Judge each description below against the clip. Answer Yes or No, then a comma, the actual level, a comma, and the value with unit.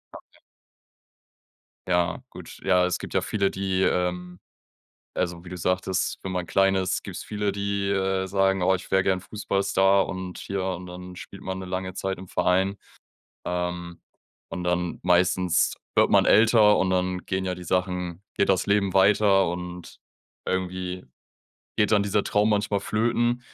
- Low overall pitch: Yes, very low, 95 Hz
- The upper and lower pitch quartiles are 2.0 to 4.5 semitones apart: No, narrow, 1.5 semitones